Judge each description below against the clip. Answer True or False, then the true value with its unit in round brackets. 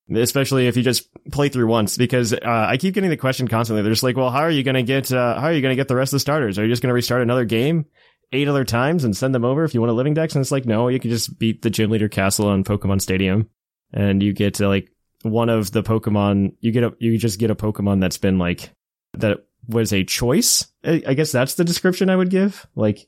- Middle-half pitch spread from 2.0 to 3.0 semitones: False (3.7 semitones)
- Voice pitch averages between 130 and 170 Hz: False (120 Hz)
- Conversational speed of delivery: False (275 wpm)